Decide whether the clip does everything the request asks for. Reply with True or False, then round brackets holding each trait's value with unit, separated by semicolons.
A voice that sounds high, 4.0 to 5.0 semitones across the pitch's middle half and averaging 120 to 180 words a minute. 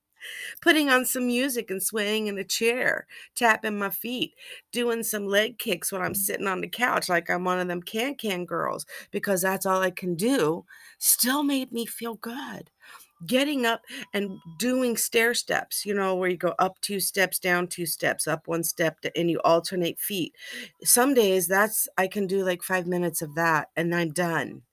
False (195 Hz; 4.7 semitones; 190 wpm)